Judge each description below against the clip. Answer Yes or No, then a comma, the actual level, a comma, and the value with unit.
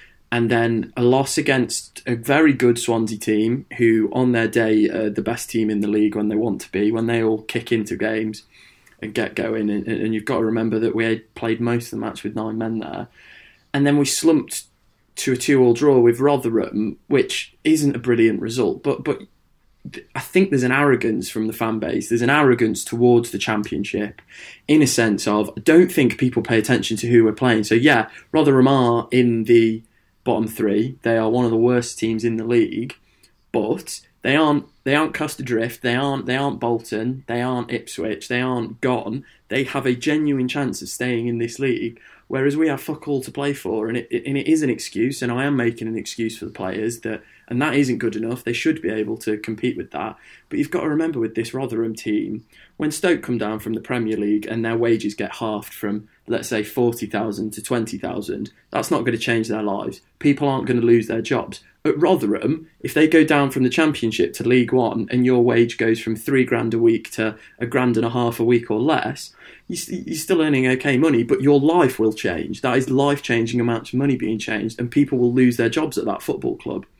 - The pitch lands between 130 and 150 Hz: No, low, 120 Hz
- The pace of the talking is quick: Yes, fast, 220 wpm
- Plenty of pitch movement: No, average, 3.0 semitones